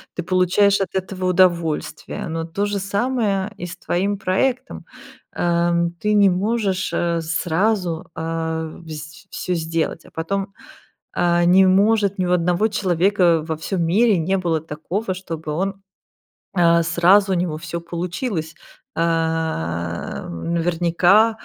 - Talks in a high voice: No, medium, 175 Hz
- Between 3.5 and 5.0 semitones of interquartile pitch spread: No, average, 3.0 semitones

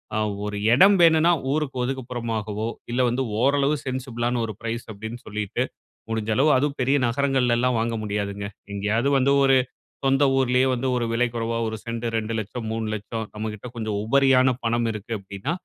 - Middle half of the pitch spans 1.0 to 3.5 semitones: Yes, average, 3.2 semitones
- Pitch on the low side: Yes, low, 120 Hz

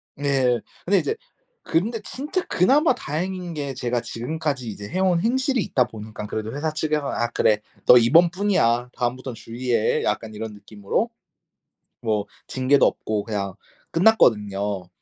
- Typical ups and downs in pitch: No, wide, 7.7 semitones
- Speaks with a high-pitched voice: No, low, 130 Hz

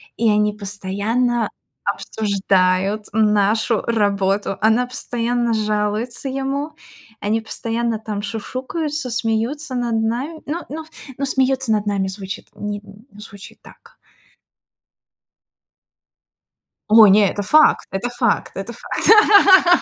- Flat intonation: No, average, 3.5 semitones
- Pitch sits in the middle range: No, high, 220 Hz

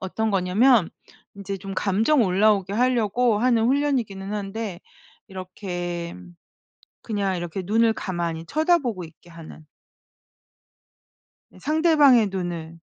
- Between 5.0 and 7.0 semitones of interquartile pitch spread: No, average, 4.4 semitones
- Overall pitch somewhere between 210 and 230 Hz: No, high, 200 Hz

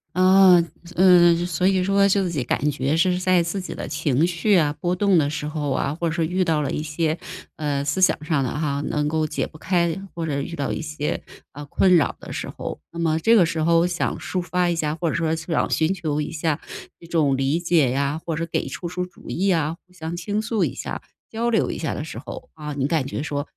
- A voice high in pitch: No, medium, 165 Hz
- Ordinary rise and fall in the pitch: Yes, average, 3.2 semitones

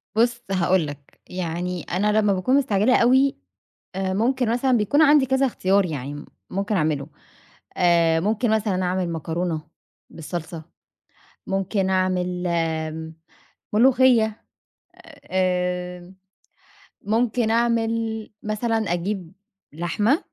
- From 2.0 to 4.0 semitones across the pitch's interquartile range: No, average, 4.6 semitones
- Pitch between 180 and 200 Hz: Yes, high, 190 Hz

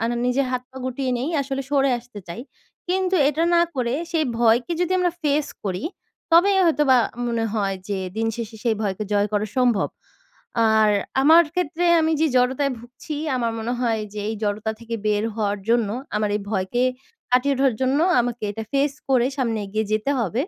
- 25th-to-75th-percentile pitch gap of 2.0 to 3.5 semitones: No, average, 4.2 semitones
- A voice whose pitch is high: Yes, high, 245 Hz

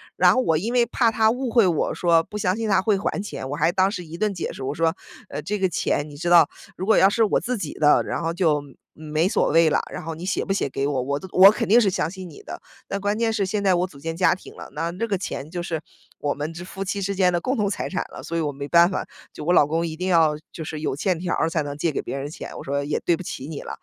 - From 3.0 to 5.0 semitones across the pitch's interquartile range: Yes, average, 4.2 semitones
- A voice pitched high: No, medium, 175 Hz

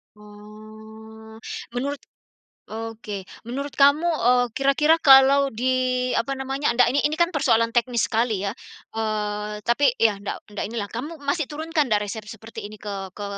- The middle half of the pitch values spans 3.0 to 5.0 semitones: Yes, average, 4.3 semitones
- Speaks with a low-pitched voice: No, high, 230 Hz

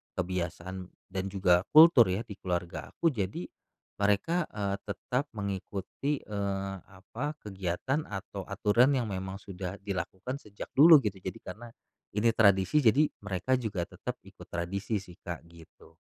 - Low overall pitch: Yes, low, 100 Hz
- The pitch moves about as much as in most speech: Yes, average, 3.7 semitones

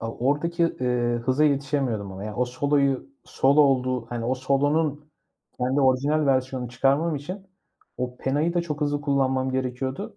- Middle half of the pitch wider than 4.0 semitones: No, average, 2.7 semitones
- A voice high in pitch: No, low, 135 Hz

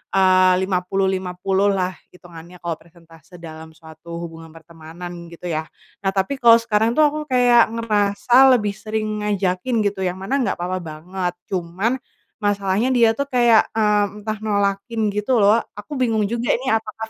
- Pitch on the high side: Yes, high, 200 Hz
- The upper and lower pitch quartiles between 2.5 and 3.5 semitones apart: No, average, 3.9 semitones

